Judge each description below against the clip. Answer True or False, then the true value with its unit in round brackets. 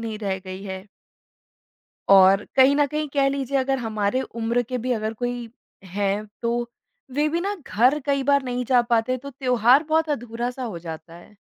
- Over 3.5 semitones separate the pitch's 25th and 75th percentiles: True (4.4 semitones)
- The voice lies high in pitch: True (245 Hz)